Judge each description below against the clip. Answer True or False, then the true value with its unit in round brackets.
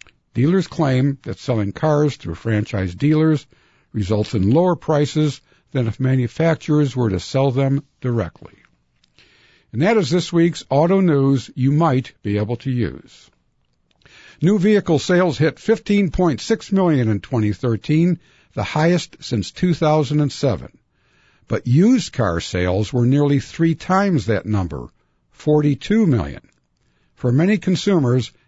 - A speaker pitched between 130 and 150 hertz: True (140 Hz)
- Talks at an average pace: False (125 wpm)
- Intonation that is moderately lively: False (6.4 semitones)